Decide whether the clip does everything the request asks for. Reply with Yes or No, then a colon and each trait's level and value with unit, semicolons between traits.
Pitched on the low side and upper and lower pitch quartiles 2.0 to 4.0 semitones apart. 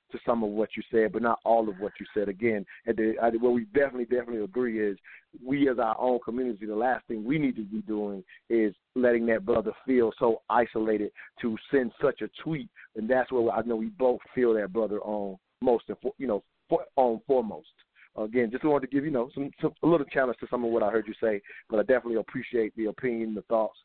Yes: low, 115 Hz; narrow, 2.6 semitones